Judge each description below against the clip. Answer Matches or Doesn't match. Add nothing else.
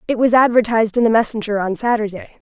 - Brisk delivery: Doesn't match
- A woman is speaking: Matches